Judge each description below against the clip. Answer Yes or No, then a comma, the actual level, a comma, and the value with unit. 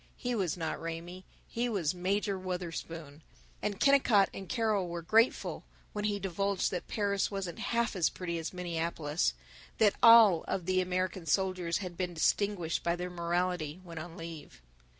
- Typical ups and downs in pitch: Yes, average, 3.0 semitones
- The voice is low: No, medium, 180 Hz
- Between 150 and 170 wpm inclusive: Yes, average, 160 wpm